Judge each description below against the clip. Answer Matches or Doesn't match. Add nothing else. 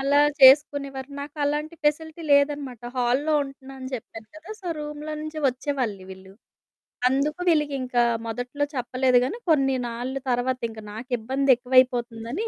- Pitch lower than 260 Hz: Doesn't match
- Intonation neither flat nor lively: Matches